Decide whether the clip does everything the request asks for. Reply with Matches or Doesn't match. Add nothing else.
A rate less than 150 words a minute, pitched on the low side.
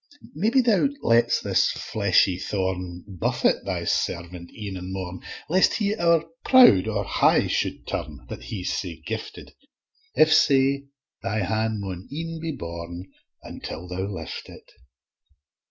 Matches